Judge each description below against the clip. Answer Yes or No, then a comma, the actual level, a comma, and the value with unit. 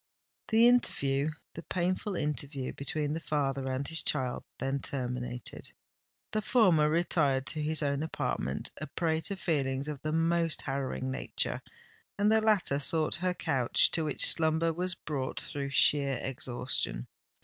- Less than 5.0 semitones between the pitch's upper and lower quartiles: Yes, average, 3.6 semitones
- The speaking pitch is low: No, medium, 150 Hz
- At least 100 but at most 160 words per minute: Yes, average, 145 wpm